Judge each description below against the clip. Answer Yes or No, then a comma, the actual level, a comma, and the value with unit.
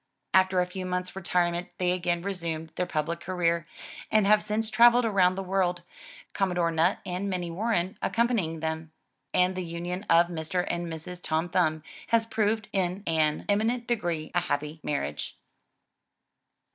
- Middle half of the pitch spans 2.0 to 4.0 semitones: Yes, average, 2.8 semitones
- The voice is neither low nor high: Yes, medium, 180 Hz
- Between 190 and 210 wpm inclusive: No, average, 160 wpm